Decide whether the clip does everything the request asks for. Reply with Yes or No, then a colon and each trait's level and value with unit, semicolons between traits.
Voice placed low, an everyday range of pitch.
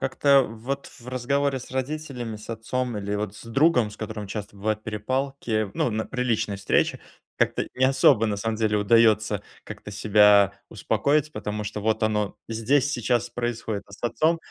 Yes: low, 115 Hz; average, 3.5 semitones